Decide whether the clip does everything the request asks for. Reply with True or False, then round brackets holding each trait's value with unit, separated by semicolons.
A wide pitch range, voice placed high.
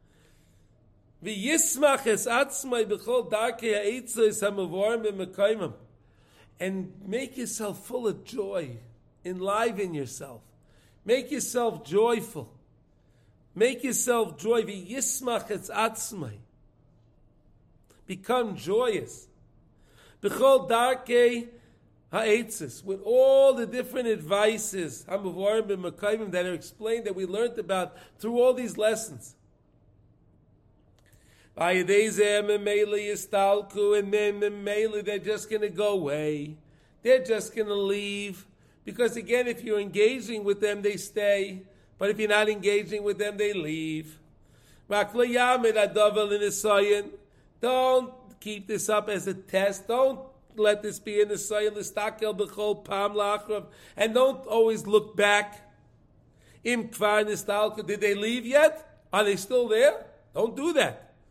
False (3.1 semitones; 210 Hz)